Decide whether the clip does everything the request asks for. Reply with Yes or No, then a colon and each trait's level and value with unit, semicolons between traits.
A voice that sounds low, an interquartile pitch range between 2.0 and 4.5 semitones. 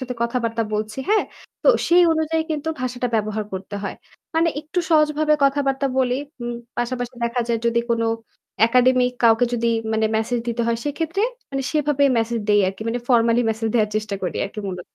No: high, 245 Hz; average, 4.0 semitones